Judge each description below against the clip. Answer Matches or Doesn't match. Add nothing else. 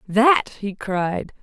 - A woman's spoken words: Matches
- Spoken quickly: Doesn't match